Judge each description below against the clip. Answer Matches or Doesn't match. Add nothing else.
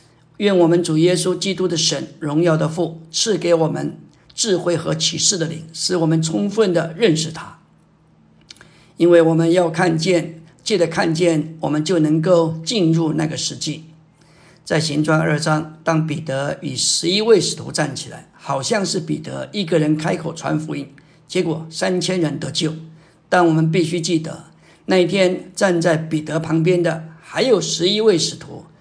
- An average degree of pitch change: Doesn't match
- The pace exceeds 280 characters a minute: Doesn't match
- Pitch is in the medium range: Matches